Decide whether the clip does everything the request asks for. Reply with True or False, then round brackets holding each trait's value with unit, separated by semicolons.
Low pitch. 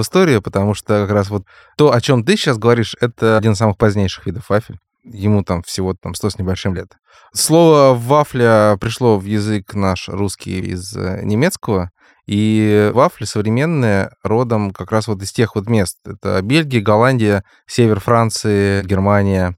True (105 Hz)